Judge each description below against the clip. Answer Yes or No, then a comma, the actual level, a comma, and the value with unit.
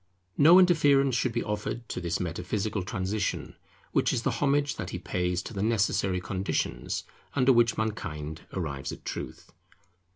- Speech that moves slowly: No, average, 155 wpm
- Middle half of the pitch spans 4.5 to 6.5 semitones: Yes, wide, 5.6 semitones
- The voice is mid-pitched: No, low, 105 Hz